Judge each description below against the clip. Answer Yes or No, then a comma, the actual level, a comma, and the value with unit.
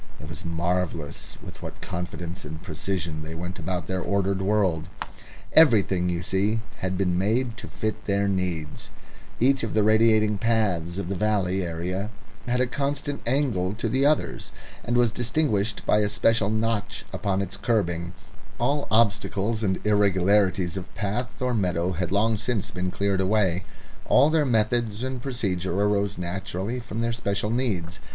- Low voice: Yes, low, 100 Hz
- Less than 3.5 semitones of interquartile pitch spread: No, average, 3.8 semitones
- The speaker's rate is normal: Yes, average, 160 wpm